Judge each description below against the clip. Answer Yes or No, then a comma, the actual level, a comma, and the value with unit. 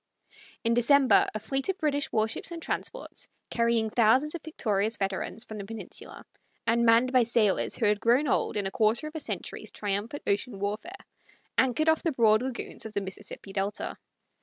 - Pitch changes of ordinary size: Yes, average, 4.3 semitones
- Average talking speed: Yes, average, 185 wpm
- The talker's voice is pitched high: Yes, high, 230 Hz